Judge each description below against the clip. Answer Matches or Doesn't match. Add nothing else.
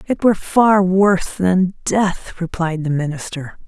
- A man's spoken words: Doesn't match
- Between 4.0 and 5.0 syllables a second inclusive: Matches